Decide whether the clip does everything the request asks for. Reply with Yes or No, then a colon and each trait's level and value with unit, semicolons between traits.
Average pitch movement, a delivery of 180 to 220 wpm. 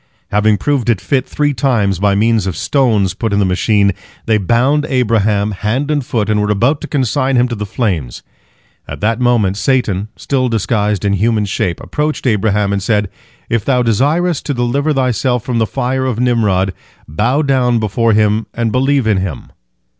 Yes: average, 3.9 semitones; average, 185 wpm